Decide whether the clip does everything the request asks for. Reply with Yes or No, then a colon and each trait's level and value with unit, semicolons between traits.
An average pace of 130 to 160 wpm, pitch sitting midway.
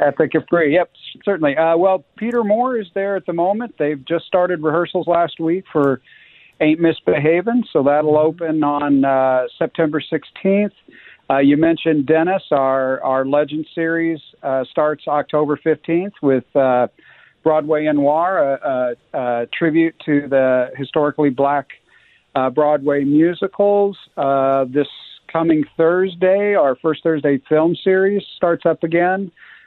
Yes: average, 140 wpm; medium, 160 Hz